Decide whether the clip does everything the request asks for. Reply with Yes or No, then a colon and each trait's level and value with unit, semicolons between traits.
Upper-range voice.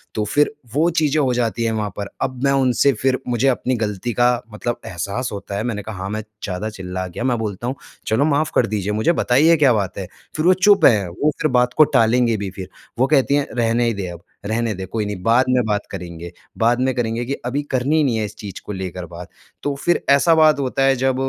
No: low, 120 Hz